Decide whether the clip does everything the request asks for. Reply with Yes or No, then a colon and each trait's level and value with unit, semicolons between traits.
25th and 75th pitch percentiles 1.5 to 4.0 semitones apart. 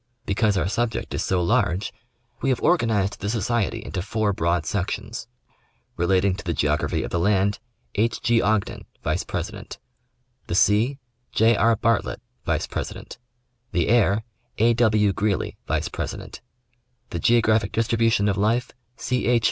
Yes: average, 3.1 semitones